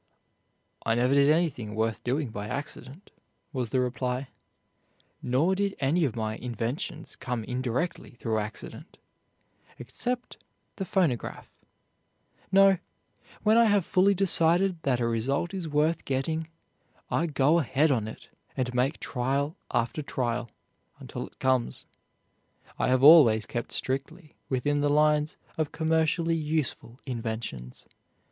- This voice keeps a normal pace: No, slow, 130 wpm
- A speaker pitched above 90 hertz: Yes, medium, 140 Hz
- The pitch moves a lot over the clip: No, average, 4.9 semitones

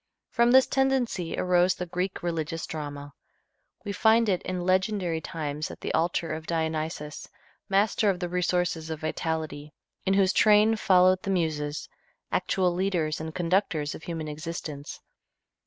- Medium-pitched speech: Yes, medium, 175 Hz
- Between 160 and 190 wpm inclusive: No, average, 145 wpm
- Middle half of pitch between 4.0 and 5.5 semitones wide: No, average, 3.4 semitones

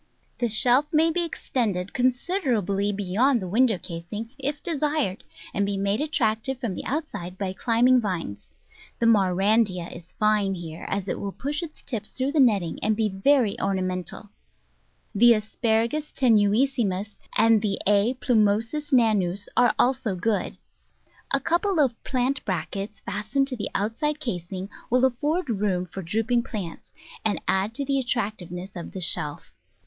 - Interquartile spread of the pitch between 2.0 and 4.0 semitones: No, average, 5.0 semitones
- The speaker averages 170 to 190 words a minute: No, average, 155 wpm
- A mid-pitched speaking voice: No, high, 220 Hz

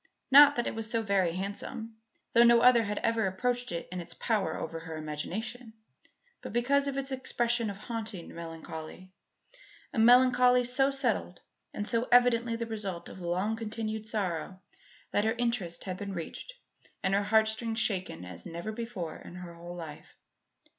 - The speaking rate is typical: Yes, average, 165 wpm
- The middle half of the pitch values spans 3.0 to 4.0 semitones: No, average, 4.7 semitones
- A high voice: Yes, high, 220 Hz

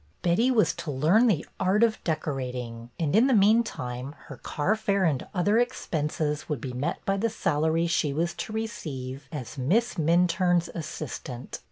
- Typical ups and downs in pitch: No, wide, 6.6 semitones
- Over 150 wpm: Yes, average, 160 wpm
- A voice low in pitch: No, medium, 165 Hz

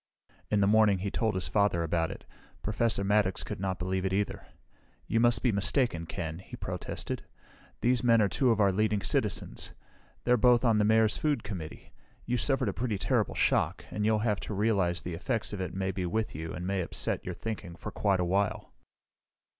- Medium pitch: No, low, 105 Hz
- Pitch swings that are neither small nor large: Yes, average, 3.1 semitones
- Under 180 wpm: No, average, 200 wpm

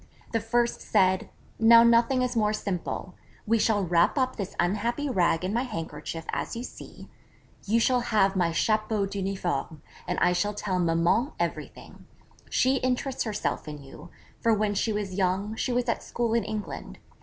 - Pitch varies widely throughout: No, average, 4.1 semitones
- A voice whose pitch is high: Yes, high, 210 Hz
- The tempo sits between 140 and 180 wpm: Yes, average, 170 wpm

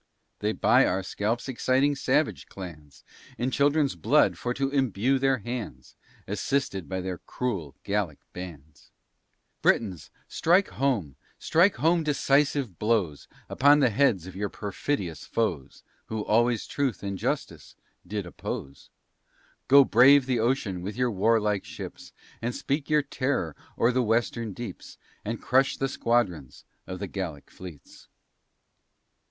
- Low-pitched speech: Yes, low, 115 Hz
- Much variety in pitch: Yes, wide, 6.3 semitones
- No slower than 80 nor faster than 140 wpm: Yes, slow, 135 wpm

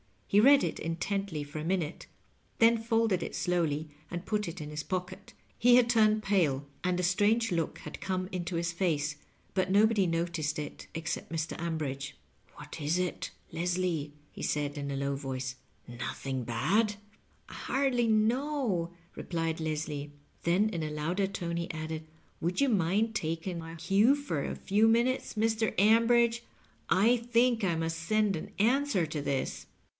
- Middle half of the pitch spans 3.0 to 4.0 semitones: No, wide, 5.6 semitones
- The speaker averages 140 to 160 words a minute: No, average, 170 wpm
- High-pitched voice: No, medium, 175 Hz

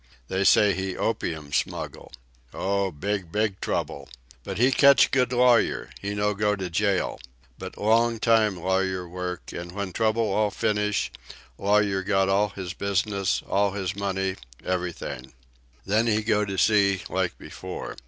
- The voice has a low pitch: Yes, low, 100 Hz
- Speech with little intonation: Yes, narrow, 2.0 semitones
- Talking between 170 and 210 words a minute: No, average, 150 wpm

